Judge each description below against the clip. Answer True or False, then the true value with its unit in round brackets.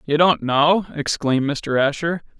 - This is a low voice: False (150 Hz)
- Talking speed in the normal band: True (150 wpm)